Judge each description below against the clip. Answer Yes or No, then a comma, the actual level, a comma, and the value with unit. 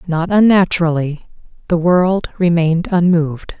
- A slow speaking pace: Yes, slow, 100 wpm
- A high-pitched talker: No, medium, 170 Hz